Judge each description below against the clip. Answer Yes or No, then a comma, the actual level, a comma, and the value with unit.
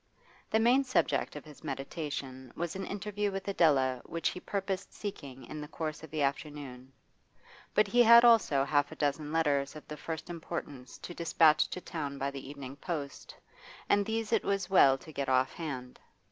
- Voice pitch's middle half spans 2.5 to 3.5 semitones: No, wide, 5.5 semitones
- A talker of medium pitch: Yes, medium, 155 Hz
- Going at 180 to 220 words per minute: Yes, average, 185 wpm